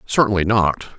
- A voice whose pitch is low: Yes, low, 100 Hz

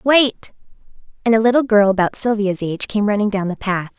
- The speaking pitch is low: No, high, 210 Hz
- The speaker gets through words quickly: No, average, 195 wpm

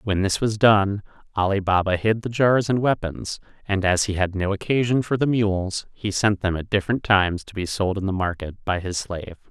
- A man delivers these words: Yes, male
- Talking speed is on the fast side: Yes, fast, 220 wpm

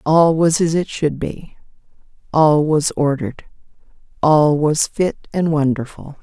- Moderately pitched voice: Yes, medium, 150 Hz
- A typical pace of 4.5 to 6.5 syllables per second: No, 3.9 syllables/s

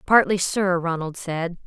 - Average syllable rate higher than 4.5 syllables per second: No, 4.1 syllables/s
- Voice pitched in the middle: Yes, medium, 180 Hz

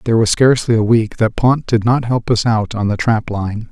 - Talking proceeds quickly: Yes, fast, 260 wpm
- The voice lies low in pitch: Yes, low, 115 Hz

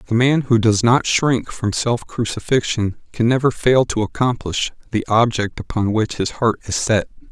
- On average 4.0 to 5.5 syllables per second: Yes, 4.6 syllables/s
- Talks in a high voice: No, low, 115 Hz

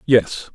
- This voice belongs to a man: Yes, male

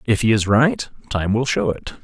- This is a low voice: Yes, low, 115 Hz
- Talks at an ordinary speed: No, fast, 235 wpm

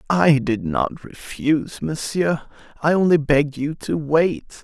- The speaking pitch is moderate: Yes, medium, 155 Hz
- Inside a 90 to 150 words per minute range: Yes, average, 140 wpm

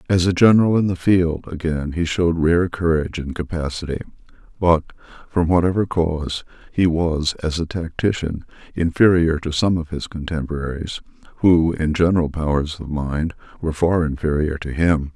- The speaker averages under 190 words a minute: Yes, average, 155 wpm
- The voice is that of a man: Yes, male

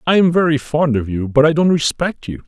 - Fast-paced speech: Yes, fast, 265 wpm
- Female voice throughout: No, male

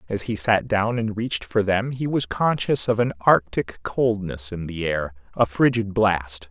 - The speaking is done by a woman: No, male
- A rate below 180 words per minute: No, average, 195 wpm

